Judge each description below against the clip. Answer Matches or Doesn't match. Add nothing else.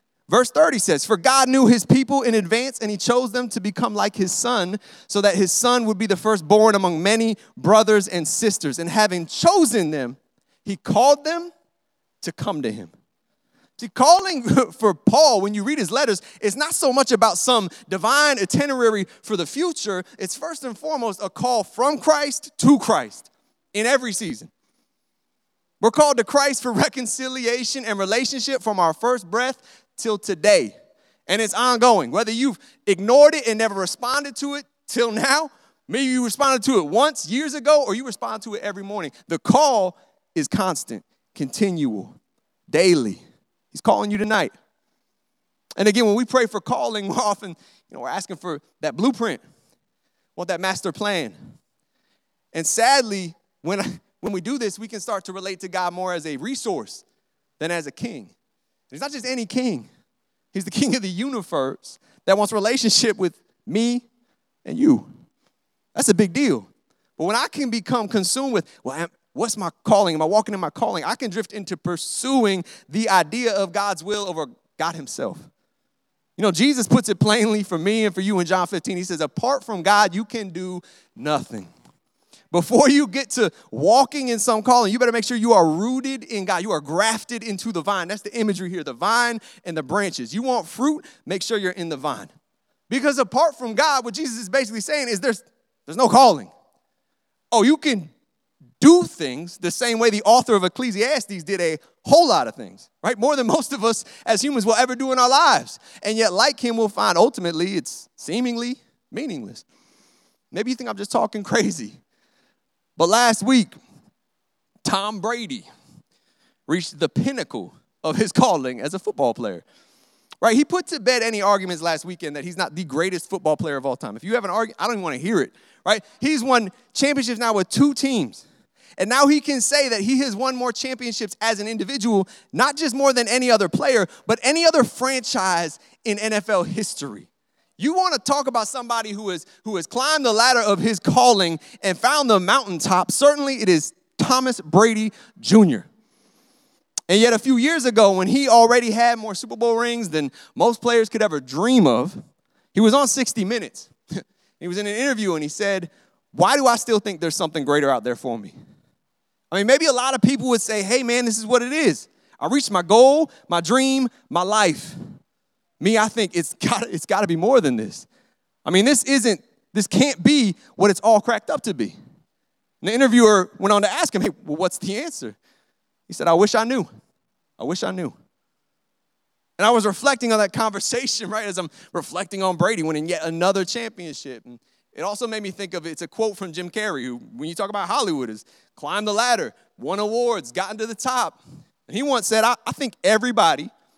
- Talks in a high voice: Matches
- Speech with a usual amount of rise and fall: Matches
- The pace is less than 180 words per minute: Doesn't match